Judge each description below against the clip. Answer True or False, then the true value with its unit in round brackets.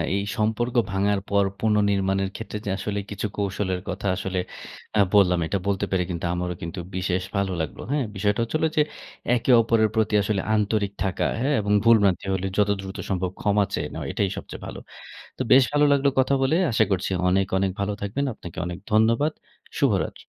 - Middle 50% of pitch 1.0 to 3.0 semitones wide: True (2.5 semitones)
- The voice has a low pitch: True (100 Hz)